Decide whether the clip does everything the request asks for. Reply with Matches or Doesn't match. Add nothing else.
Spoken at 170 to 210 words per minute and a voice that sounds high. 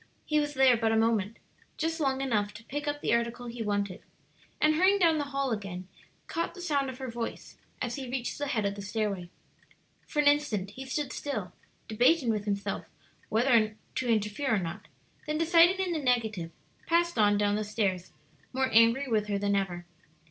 Matches